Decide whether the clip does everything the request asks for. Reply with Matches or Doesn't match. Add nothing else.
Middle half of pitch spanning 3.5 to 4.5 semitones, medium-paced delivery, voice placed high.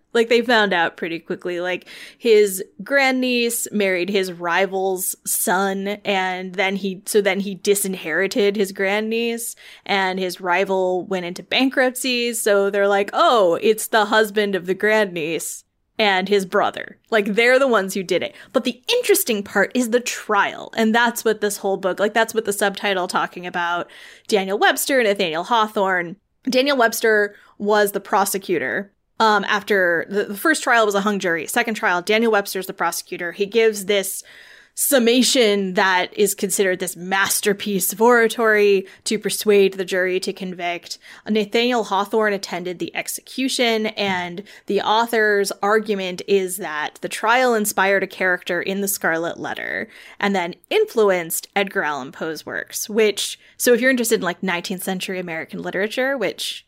Doesn't match